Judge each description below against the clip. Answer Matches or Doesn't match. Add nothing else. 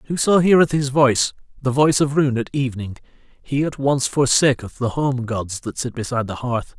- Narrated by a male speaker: Matches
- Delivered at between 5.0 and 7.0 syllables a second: Matches